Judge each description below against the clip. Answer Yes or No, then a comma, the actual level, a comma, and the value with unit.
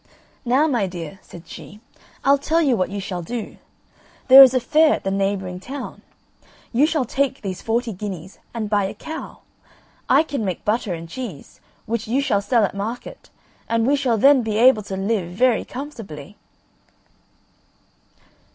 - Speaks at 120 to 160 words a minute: No, average, 170 wpm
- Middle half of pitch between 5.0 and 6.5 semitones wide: Yes, average, 5.3 semitones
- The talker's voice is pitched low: No, high, 225 Hz